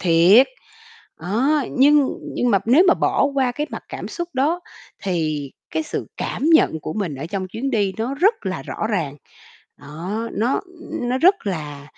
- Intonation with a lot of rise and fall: Yes, wide, 8.2 semitones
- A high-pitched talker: Yes, high, 220 Hz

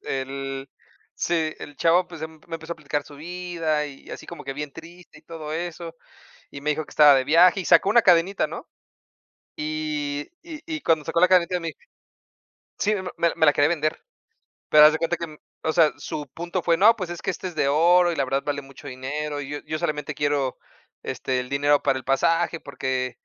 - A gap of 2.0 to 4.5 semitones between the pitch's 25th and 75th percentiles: Yes, average, 3.0 semitones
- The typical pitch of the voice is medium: Yes, medium, 155 Hz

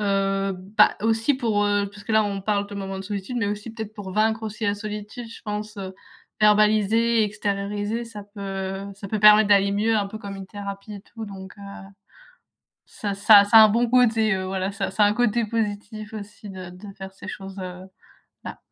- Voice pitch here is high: Yes, high, 205 Hz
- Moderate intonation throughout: No, narrow, 1.7 semitones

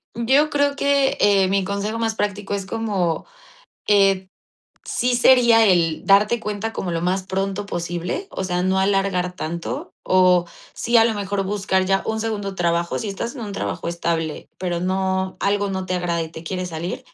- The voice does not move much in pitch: No, average, 3.0 semitones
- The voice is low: No, high, 195 Hz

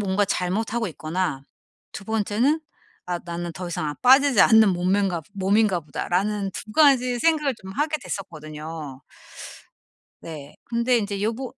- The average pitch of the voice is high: Yes, high, 200 Hz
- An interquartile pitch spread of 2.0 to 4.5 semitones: No, average, 5.2 semitones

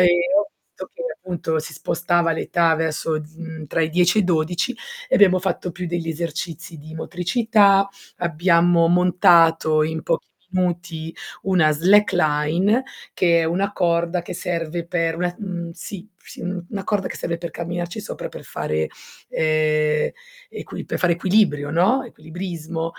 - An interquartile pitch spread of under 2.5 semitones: Yes, narrow, 1.9 semitones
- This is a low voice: No, medium, 170 Hz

